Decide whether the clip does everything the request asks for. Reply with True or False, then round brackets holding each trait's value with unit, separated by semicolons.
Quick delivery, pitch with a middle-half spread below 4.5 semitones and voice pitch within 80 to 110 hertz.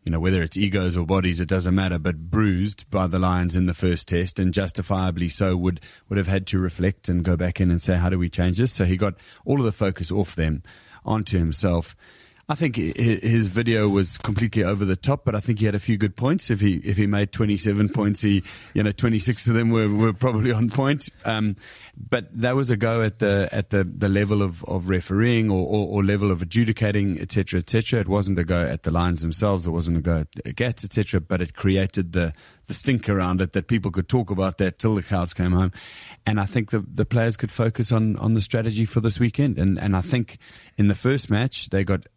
True (245 wpm; 3.5 semitones; 100 Hz)